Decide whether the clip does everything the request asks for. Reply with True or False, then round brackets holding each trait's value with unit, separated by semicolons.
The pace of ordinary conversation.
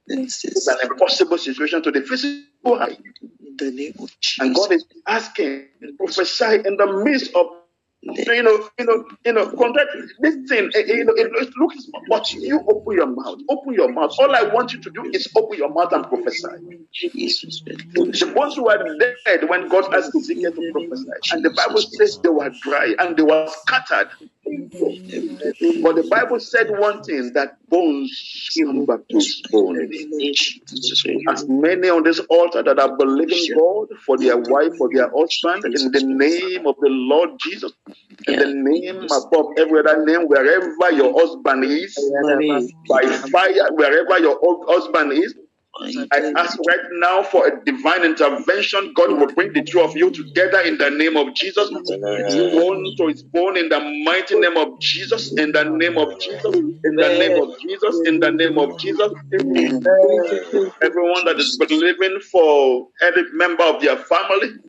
True (170 wpm)